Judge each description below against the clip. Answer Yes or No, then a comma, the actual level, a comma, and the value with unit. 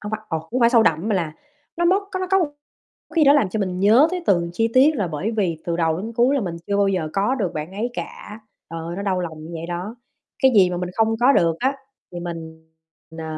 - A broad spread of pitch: Yes, wide, 5.9 semitones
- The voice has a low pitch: No, high, 200 Hz